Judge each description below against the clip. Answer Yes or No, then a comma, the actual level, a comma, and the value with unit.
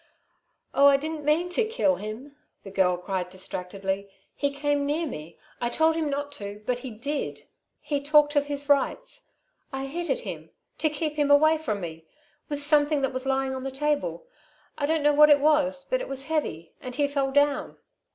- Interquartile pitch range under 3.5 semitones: Yes, average, 3.0 semitones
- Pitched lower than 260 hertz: No, very high, 285 Hz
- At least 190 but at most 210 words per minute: Yes, average, 200 wpm